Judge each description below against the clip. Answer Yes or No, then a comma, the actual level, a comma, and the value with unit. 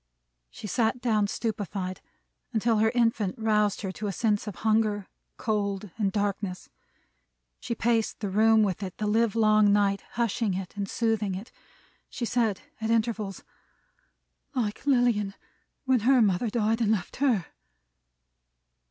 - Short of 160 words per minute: Yes, average, 140 wpm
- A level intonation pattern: Yes, narrow, 2.2 semitones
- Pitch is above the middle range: Yes, high, 215 Hz